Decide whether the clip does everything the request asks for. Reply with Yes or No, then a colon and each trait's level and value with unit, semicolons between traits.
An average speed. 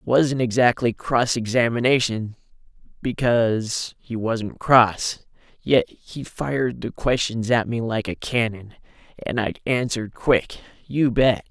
No: slow, 130 wpm